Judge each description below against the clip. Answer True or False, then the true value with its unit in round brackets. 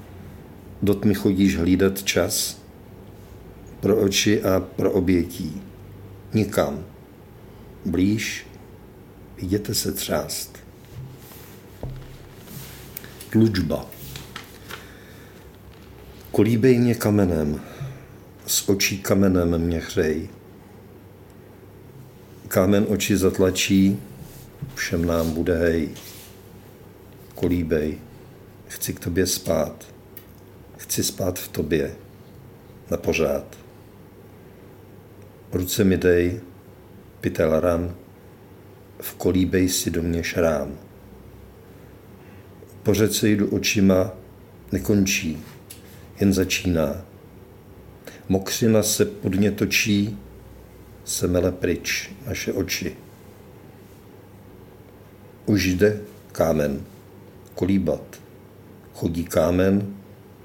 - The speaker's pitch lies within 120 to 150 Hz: False (95 Hz)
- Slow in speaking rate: True (75 wpm)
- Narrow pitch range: True (2.0 semitones)